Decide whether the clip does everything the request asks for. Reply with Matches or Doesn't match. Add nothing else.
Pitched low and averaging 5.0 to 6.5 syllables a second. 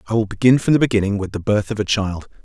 Doesn't match